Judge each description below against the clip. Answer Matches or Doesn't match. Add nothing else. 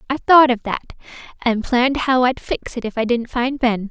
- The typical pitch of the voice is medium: Doesn't match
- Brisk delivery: Matches